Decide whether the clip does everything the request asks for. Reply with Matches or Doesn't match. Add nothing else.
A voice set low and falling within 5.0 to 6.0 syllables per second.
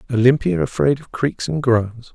Doesn't match